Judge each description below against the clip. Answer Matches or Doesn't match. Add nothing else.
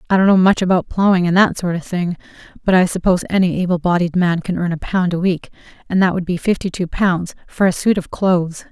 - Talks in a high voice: Doesn't match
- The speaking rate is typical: Doesn't match